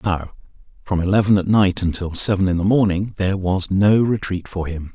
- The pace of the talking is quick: No, average, 195 wpm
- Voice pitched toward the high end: No, very low, 95 Hz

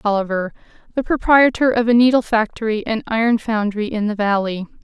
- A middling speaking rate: Yes, average, 160 wpm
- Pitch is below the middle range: No, high, 225 Hz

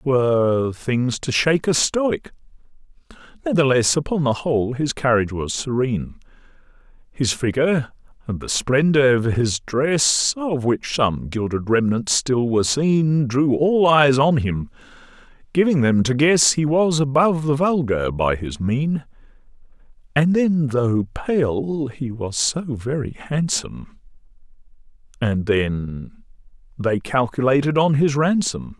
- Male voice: Yes, male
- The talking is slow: Yes, slow, 130 wpm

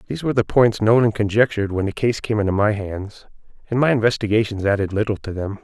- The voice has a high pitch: No, low, 105 Hz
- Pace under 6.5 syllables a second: No, 6.6 syllables/s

